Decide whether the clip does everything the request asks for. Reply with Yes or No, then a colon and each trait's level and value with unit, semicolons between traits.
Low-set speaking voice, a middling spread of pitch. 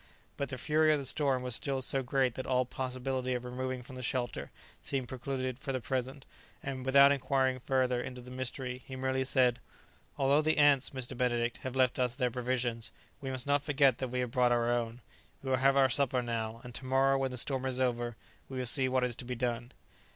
No: low, 130 Hz; narrow, 1.3 semitones